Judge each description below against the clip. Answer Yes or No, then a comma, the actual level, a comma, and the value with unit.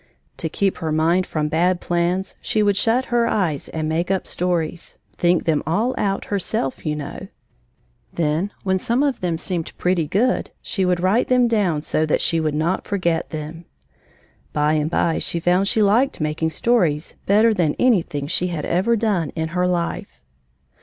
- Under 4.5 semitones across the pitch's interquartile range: Yes, average, 4.1 semitones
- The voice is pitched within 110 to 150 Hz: No, medium, 175 Hz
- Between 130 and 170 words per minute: No, average, 180 wpm